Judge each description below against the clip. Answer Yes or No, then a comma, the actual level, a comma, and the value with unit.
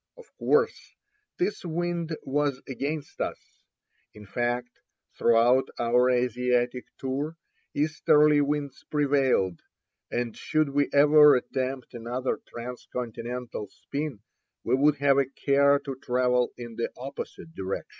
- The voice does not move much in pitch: No, average, 3.1 semitones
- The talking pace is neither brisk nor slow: No, slow, 115 wpm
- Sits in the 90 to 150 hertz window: Yes, low, 135 Hz